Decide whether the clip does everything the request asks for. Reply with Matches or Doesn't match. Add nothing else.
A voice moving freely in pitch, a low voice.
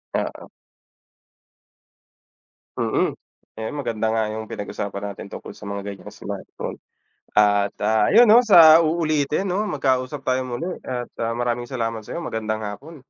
Matches